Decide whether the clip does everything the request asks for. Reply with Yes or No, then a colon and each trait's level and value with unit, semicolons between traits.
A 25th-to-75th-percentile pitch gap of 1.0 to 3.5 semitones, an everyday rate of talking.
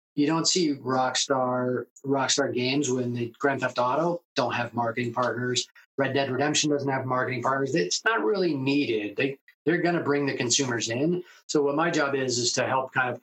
Yes: narrow, 2.5 semitones; average, 195 wpm